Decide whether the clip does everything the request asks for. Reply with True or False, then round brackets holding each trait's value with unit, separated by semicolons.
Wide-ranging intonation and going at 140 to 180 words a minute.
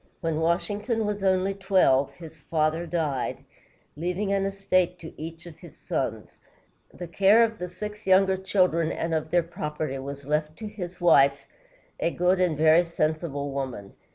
False (3.7 semitones; 160 wpm)